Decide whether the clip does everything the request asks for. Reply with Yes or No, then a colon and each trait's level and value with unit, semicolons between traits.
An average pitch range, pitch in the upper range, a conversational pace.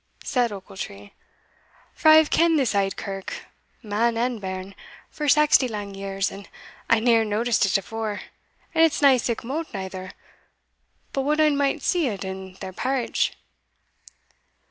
No: wide, 6.1 semitones; high, 225 Hz; average, 150 wpm